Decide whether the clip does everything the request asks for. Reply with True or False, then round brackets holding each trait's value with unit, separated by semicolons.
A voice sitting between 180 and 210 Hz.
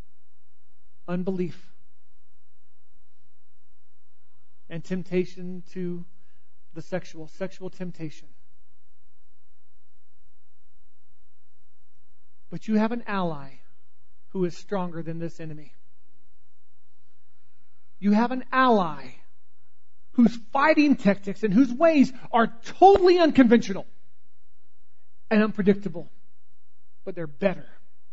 False (150 Hz)